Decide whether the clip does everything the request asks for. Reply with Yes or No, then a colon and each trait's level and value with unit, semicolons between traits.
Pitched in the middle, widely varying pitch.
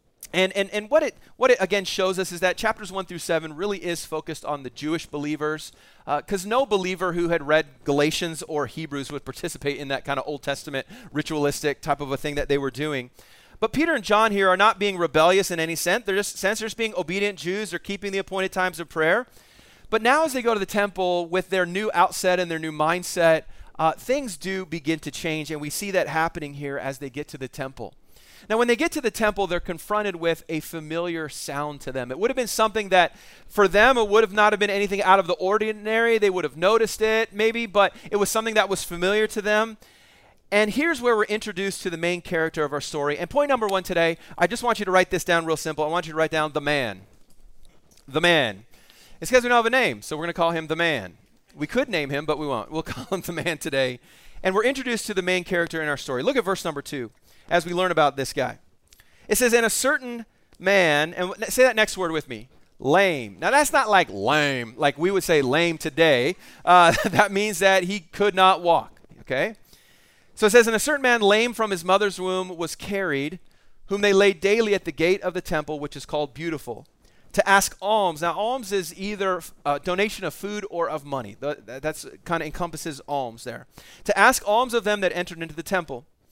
No: medium, 180 Hz; average, 5.0 semitones